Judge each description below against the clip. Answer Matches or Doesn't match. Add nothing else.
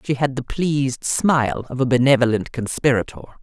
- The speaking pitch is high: Doesn't match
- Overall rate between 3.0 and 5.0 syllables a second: Doesn't match